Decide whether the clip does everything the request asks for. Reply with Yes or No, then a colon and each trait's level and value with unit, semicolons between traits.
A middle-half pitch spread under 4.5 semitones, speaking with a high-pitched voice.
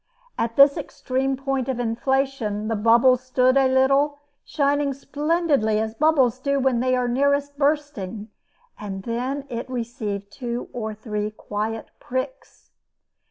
Yes: average, 3.6 semitones; very high, 255 Hz